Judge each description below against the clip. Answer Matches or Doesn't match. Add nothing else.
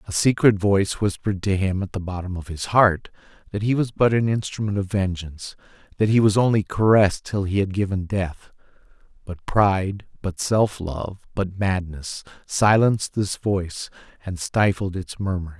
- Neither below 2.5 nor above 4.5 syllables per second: Doesn't match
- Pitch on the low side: Matches